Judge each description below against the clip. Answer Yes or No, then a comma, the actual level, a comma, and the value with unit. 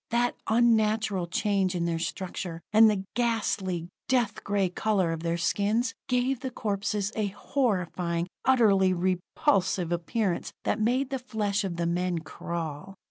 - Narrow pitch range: No, average, 4.1 semitones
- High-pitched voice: Yes, high, 200 Hz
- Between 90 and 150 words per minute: Yes, average, 140 wpm